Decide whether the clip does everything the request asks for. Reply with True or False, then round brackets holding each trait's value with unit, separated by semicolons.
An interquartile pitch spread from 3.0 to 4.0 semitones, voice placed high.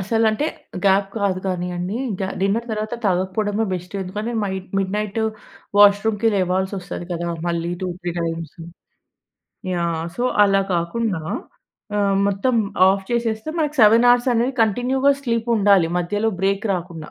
True (3.4 semitones; 200 Hz)